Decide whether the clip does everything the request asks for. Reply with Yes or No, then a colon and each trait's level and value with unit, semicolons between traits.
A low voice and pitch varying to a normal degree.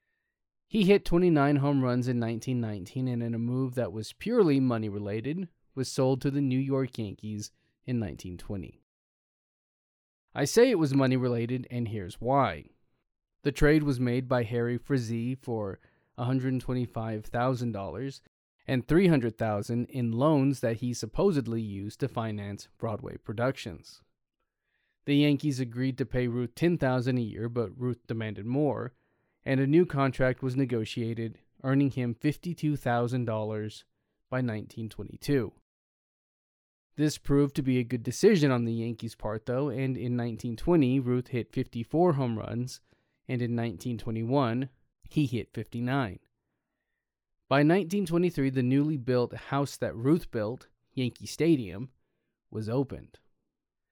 Yes: low, 125 Hz; average, 3.3 semitones